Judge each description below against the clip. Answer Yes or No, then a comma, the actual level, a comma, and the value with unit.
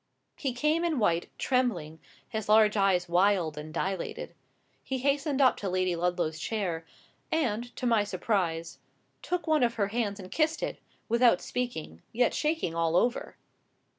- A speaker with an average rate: Yes, average, 155 wpm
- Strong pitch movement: Yes, wide, 6.1 semitones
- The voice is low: No, high, 210 Hz